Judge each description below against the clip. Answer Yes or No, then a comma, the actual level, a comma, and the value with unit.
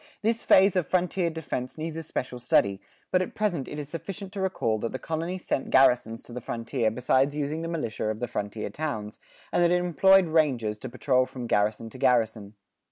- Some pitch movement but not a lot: No, wide, 6.7 semitones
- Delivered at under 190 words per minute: No, fast, 205 wpm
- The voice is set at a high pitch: No, low, 135 Hz